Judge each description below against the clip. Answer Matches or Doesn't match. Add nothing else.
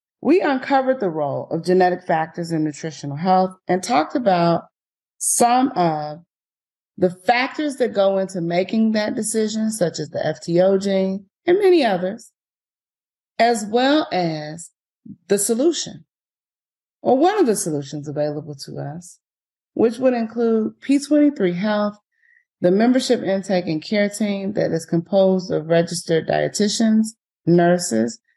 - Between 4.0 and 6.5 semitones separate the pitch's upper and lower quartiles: Matches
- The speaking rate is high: Doesn't match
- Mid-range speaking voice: Doesn't match